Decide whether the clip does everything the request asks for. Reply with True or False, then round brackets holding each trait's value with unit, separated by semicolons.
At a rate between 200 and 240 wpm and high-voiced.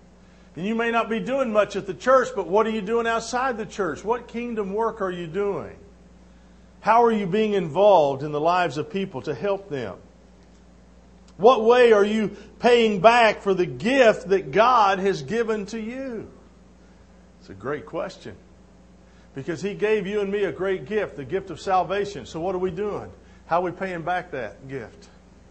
False (190 wpm; 200 Hz)